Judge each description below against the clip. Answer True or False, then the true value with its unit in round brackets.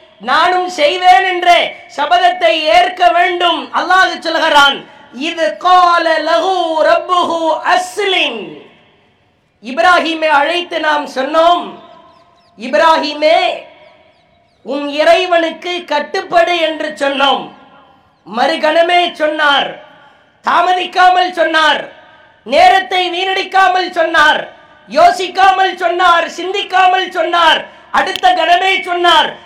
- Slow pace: True (75 wpm)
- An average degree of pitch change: False (2.3 semitones)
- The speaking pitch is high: True (335 Hz)